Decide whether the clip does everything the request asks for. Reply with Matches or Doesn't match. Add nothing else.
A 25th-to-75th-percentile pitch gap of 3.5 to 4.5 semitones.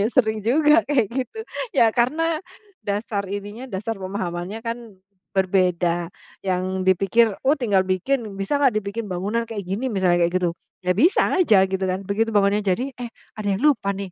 Matches